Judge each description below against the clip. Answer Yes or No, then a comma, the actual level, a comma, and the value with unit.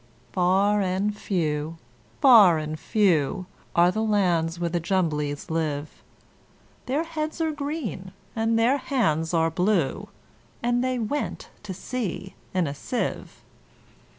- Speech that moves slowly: Yes, slow, 125 wpm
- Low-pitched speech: No, high, 190 Hz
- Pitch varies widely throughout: Yes, wide, 5.8 semitones